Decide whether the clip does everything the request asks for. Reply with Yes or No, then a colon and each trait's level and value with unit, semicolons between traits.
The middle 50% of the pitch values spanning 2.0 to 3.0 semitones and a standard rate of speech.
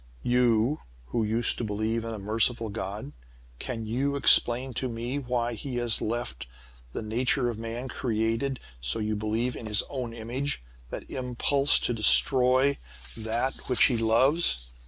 Yes: narrow, 2.4 semitones; average, 155 wpm